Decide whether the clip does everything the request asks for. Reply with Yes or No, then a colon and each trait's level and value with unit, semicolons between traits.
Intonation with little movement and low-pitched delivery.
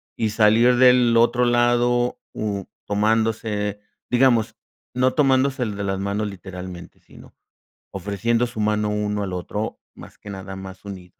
No: average, 3.3 semitones; low, 105 Hz